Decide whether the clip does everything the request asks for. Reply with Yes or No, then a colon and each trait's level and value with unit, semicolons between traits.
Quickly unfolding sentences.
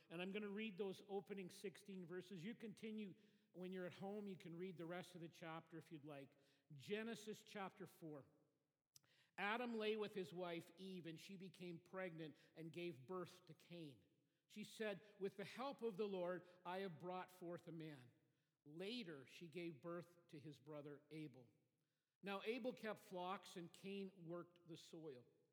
No: average, 175 wpm